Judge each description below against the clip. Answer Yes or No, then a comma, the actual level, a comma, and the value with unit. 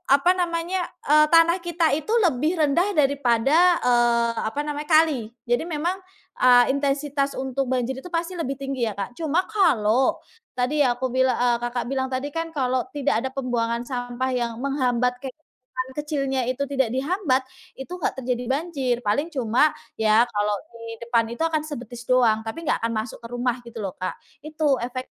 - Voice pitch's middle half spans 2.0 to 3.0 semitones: No, average, 3.7 semitones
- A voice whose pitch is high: Yes, very high, 260 Hz